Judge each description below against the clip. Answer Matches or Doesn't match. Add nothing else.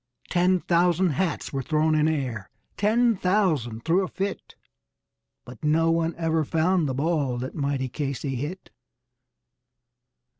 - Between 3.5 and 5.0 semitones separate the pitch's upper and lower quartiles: Matches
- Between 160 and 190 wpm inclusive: Doesn't match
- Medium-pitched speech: Matches